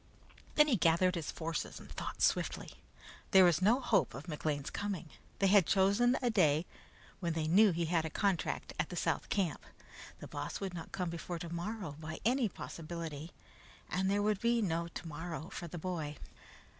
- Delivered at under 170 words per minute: No, average, 180 wpm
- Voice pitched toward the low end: No, medium, 175 Hz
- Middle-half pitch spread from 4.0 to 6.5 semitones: No, average, 3.5 semitones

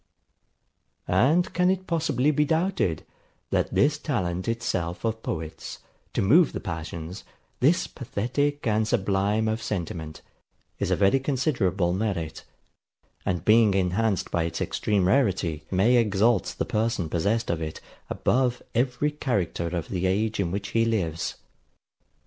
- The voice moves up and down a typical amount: No, wide, 6.0 semitones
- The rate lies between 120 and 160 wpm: Yes, slow, 135 wpm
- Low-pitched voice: Yes, low, 105 Hz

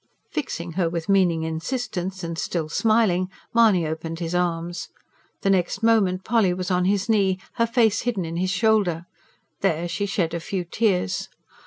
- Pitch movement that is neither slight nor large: Yes, average, 3.4 semitones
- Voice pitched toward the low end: No, medium, 185 Hz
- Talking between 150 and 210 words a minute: Yes, average, 165 wpm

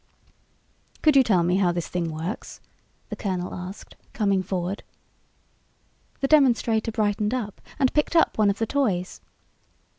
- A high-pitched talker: Yes, high, 205 Hz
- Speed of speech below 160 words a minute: Yes, average, 145 wpm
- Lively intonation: No, average, 4.7 semitones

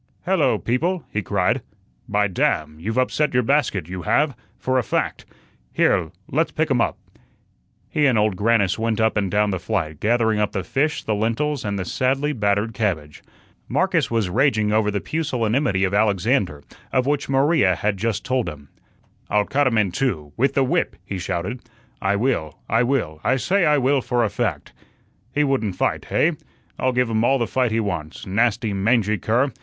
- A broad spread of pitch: No, average, 4.7 semitones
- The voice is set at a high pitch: No, low, 110 Hz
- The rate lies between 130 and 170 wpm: No, average, 185 wpm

